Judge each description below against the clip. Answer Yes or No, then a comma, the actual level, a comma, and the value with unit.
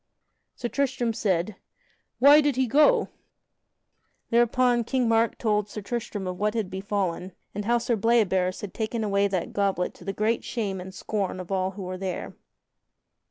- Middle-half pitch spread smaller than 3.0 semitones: No, average, 3.8 semitones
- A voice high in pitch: Yes, high, 210 Hz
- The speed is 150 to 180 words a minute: Yes, average, 170 wpm